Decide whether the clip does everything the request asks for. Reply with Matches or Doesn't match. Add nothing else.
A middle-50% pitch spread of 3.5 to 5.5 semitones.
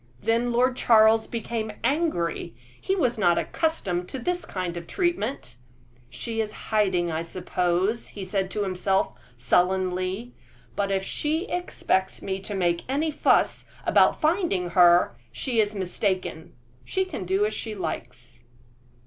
Matches